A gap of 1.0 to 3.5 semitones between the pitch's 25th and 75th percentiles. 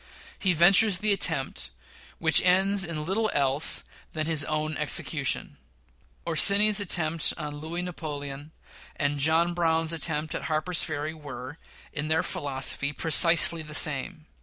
Yes: average, 2.8 semitones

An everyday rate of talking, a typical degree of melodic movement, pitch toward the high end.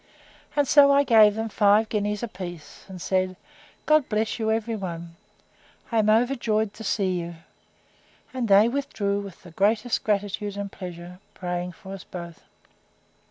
Yes: average, 160 wpm; average, 3.2 semitones; high, 205 Hz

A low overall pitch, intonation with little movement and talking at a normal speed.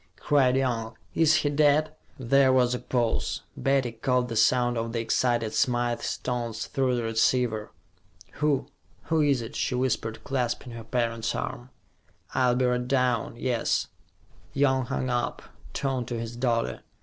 Yes: low, 125 Hz; narrow, 2.2 semitones; average, 150 wpm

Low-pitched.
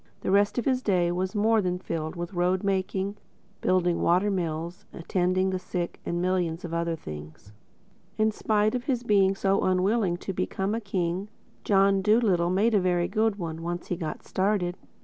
No: medium, 185 Hz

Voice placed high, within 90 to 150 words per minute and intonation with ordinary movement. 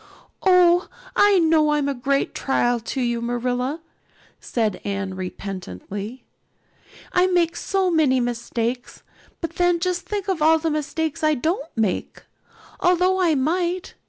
No: very high, 300 Hz; slow, 135 wpm; wide, 6.5 semitones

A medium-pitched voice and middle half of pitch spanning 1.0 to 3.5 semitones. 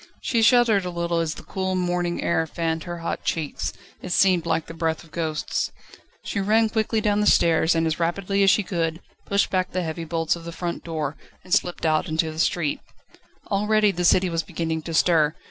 Yes: medium, 170 Hz; average, 2.9 semitones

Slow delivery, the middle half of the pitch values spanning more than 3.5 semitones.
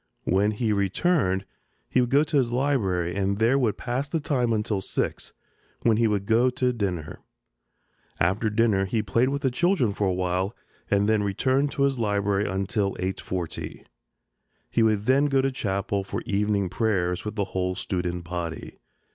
No: average, 170 wpm; average, 4.5 semitones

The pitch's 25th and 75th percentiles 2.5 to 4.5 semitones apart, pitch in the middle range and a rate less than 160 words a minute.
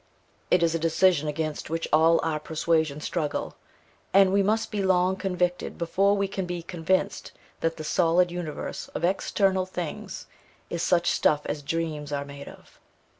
No: average, 3.1 semitones; medium, 170 Hz; average, 165 wpm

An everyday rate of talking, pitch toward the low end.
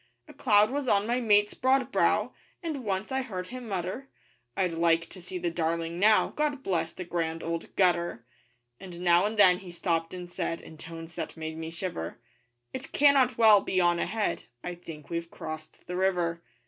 No: average, 190 wpm; medium, 180 Hz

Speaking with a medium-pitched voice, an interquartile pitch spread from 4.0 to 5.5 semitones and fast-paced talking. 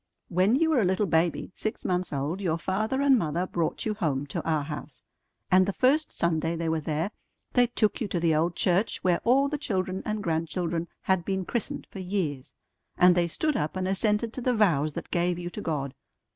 Yes: medium, 180 Hz; average, 4.5 semitones; fast, 215 wpm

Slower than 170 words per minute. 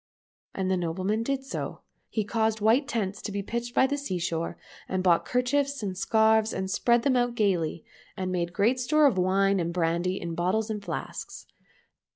No: average, 190 wpm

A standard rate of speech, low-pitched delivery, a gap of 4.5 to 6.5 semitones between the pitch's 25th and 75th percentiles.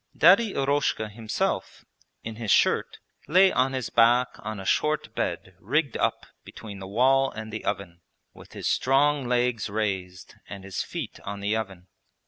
Yes: average, 160 wpm; low, 110 Hz; average, 5.0 semitones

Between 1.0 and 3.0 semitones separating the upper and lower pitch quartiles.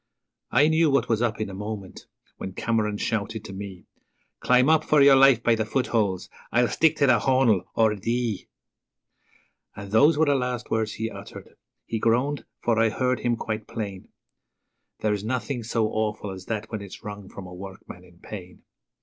No: average, 3.5 semitones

